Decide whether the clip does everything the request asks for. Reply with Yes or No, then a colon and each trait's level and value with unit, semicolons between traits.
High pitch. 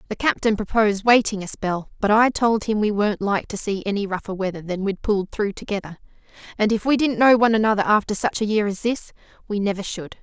Yes: high, 210 Hz